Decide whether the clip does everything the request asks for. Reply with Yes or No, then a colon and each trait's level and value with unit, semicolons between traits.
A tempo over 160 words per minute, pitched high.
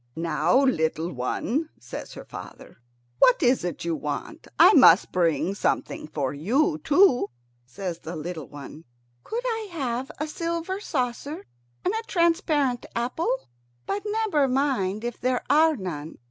No: average, 145 wpm; very high, 250 Hz